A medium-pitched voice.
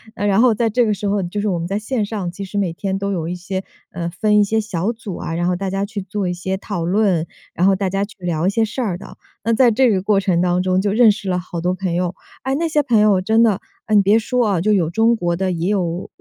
No: high, 195 Hz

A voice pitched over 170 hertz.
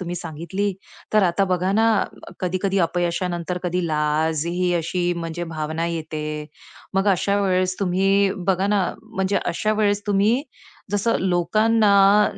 Yes: medium, 185 Hz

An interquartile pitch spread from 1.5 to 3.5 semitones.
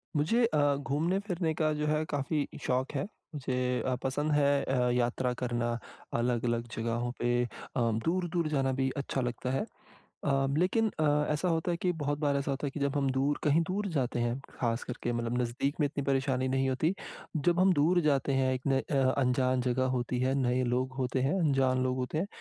Yes: average, 3.1 semitones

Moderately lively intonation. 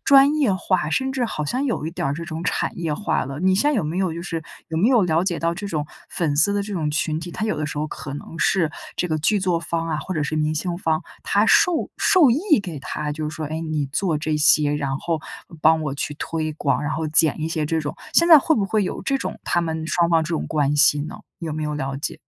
Yes: average, 3.8 semitones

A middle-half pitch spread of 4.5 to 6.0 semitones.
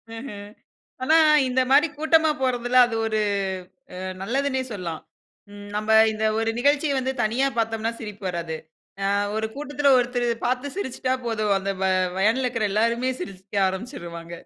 No: average, 4.1 semitones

